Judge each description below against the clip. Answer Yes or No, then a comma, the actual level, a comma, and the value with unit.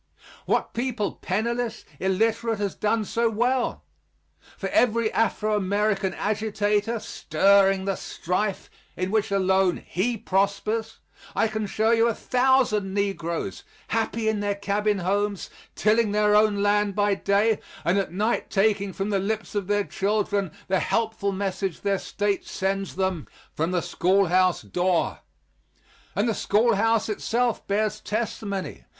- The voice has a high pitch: Yes, high, 205 Hz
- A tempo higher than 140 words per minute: No, slow, 135 wpm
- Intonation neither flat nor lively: No, narrow, 2.1 semitones